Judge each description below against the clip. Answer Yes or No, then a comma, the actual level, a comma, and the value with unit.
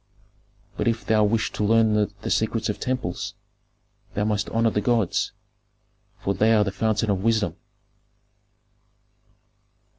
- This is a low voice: Yes, low, 110 Hz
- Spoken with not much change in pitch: Yes, narrow, 1.6 semitones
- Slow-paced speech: Yes, slow, 130 wpm